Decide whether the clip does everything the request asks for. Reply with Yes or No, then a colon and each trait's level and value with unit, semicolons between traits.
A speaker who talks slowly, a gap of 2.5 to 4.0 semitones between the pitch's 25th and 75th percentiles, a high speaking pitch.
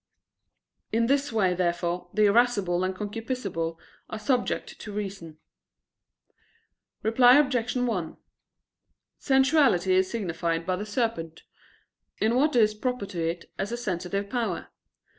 No: slow, 125 wpm; average, 5.3 semitones; high, 210 Hz